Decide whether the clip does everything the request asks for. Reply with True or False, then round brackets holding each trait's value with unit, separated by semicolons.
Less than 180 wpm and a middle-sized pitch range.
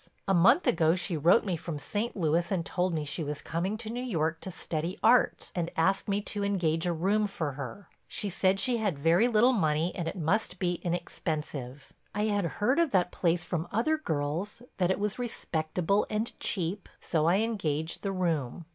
False (190 wpm; 4.2 semitones)